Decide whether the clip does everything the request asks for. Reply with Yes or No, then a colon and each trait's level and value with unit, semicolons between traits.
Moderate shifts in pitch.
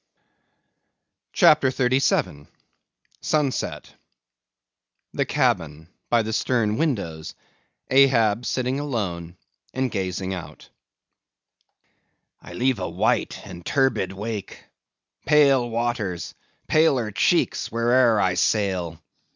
No: wide, 5.7 semitones